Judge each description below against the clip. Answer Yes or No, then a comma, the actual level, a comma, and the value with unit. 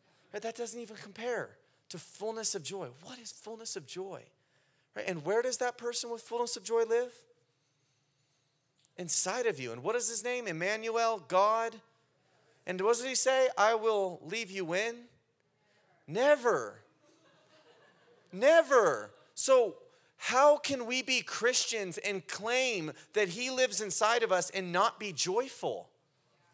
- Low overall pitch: No, high, 225 Hz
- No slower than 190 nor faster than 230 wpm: No, average, 145 wpm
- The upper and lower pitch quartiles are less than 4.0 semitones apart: No, average, 4.8 semitones